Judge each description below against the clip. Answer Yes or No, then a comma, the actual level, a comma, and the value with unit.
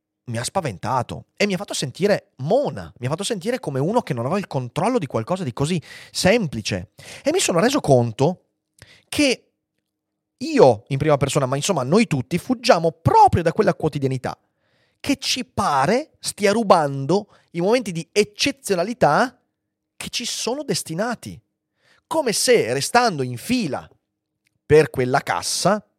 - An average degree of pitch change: No, wide, 7.8 semitones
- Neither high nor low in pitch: Yes, medium, 175 Hz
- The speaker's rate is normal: Yes, average, 150 wpm